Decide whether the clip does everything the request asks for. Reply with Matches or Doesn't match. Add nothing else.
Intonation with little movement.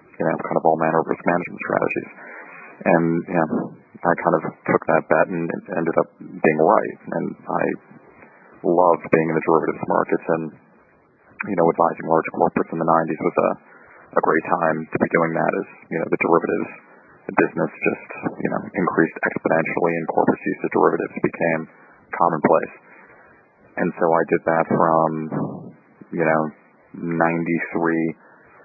Matches